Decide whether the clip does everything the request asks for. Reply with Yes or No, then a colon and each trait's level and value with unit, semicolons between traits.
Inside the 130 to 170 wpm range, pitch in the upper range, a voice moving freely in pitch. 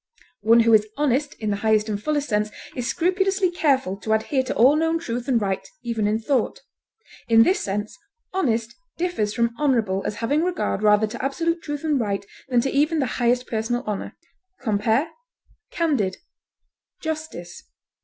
Yes: average, 165 wpm; high, 240 Hz; wide, 5.9 semitones